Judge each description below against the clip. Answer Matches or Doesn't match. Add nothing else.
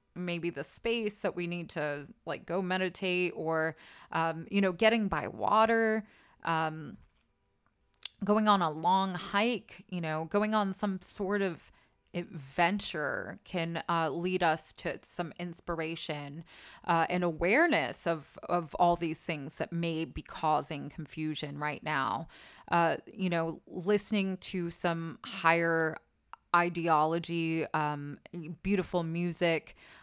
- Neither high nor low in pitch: Matches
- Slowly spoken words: Matches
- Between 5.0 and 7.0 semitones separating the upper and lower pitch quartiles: Doesn't match